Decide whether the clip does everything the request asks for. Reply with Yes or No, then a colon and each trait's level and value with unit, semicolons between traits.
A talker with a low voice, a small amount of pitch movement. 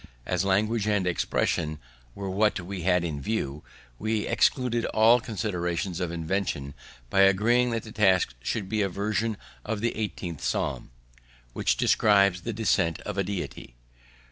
No: low, 100 Hz; average, 3.7 semitones